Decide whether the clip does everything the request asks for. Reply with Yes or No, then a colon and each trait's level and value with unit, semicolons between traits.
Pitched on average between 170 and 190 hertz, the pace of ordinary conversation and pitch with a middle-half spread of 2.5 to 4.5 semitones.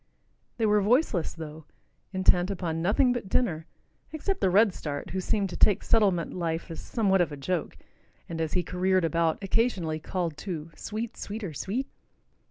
Yes: medium, 185 Hz; average, 165 wpm; average, 4.2 semitones